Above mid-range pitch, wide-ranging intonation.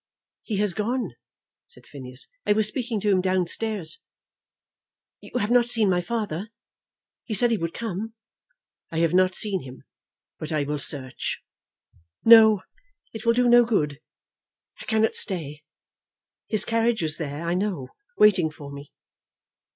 Yes: high, 195 Hz; wide, 6.0 semitones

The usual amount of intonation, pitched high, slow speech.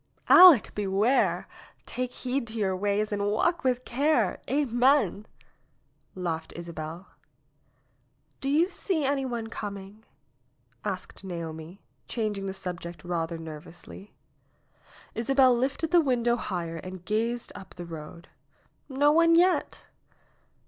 No: wide, 6.6 semitones; high, 210 Hz; slow, 120 wpm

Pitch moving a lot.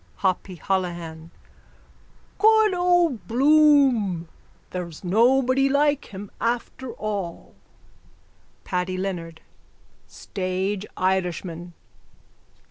Yes: wide, 6.9 semitones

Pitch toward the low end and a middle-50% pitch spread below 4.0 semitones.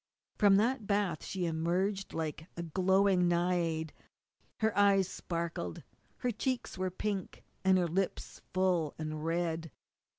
No: medium, 180 Hz; average, 3.1 semitones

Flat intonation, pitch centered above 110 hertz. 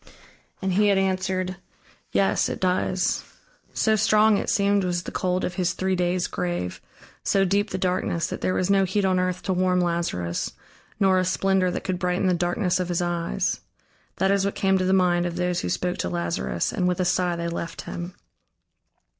Yes: narrow, 1.5 semitones; medium, 185 Hz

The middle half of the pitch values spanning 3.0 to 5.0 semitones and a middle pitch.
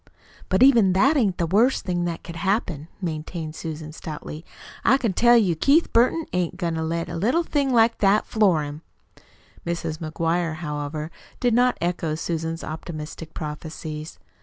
No: wide, 5.6 semitones; medium, 170 Hz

